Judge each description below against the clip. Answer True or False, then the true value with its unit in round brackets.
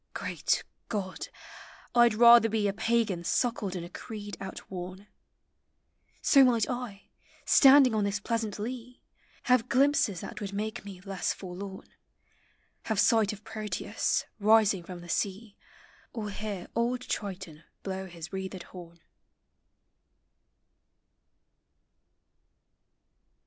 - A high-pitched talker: True (205 Hz)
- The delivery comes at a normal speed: False (120 wpm)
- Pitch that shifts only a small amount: False (3.3 semitones)